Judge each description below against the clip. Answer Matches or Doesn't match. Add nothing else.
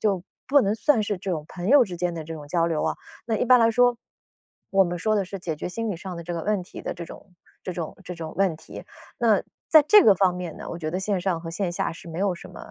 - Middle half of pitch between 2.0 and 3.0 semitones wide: Doesn't match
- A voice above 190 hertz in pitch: Doesn't match